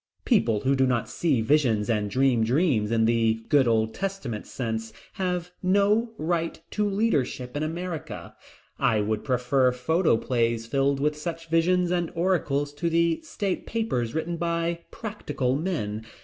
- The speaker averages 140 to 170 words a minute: Yes, average, 150 wpm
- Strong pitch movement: Yes, wide, 6.7 semitones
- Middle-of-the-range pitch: Yes, medium, 145 Hz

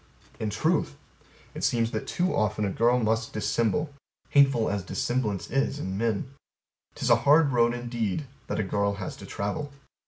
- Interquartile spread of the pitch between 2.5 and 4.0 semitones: No, average, 4.6 semitones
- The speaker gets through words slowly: No, average, 160 wpm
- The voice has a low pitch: Yes, low, 115 Hz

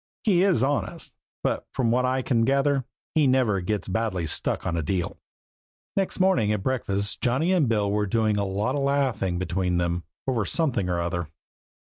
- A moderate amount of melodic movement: No, wide, 5.9 semitones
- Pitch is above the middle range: No, low, 110 Hz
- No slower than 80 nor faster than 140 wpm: No, average, 185 wpm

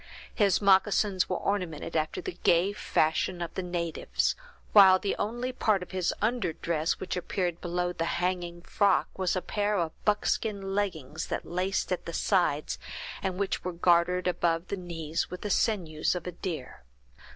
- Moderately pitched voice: Yes, medium, 180 Hz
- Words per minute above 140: Yes, average, 170 wpm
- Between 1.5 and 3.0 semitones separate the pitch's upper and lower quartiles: Yes, narrow, 2.5 semitones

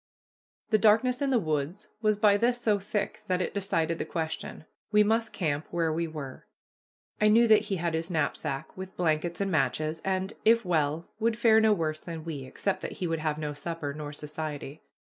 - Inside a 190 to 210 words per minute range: Yes, average, 195 wpm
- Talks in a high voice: No, medium, 170 Hz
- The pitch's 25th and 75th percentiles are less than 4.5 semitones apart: No, average, 5.2 semitones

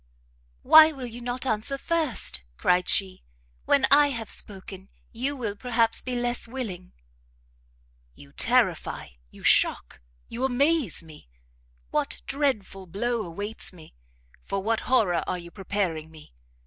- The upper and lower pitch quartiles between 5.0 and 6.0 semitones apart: Yes, wide, 5.5 semitones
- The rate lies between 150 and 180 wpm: No, slow, 135 wpm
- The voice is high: Yes, high, 225 Hz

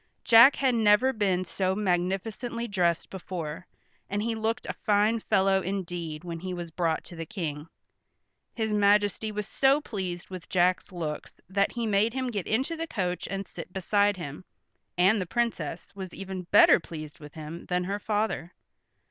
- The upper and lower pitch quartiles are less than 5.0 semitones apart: Yes, average, 3.7 semitones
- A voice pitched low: No, high, 195 Hz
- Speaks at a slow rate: No, average, 170 wpm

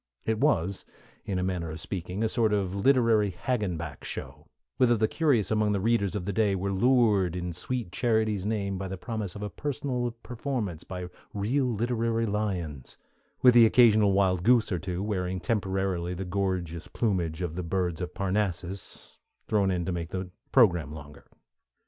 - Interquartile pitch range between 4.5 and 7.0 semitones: No, average, 3.8 semitones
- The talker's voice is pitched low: Yes, low, 100 Hz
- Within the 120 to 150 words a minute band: No, average, 175 wpm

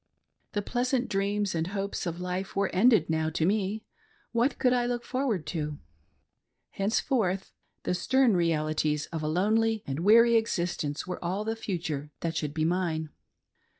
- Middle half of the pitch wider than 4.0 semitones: Yes, wide, 5.6 semitones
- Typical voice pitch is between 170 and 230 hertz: Yes, high, 190 Hz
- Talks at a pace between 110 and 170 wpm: Yes, average, 165 wpm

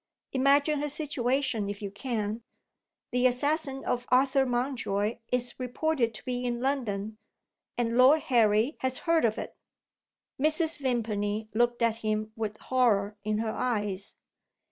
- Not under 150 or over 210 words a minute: No, average, 140 wpm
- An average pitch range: Yes, average, 3.7 semitones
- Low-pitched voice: No, high, 245 Hz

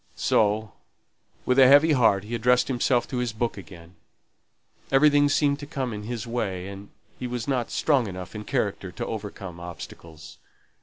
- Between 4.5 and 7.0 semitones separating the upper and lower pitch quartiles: Yes, average, 5.0 semitones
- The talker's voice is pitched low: Yes, low, 120 Hz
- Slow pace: No, average, 165 wpm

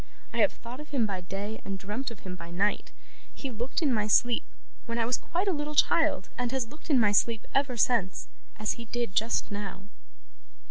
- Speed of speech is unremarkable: No, fast, 215 wpm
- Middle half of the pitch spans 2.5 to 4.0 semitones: No, average, 4.5 semitones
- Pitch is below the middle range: No, high, 230 Hz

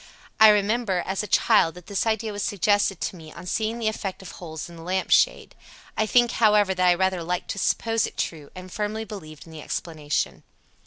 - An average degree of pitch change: Yes, average, 3.7 semitones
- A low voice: No, high, 190 Hz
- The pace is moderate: No, fast, 215 wpm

